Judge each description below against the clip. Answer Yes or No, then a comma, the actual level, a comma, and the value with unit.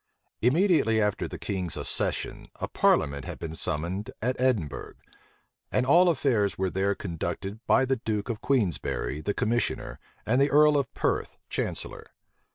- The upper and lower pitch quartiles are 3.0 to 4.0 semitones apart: No, wide, 5.6 semitones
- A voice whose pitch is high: No, low, 110 Hz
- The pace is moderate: Yes, average, 150 wpm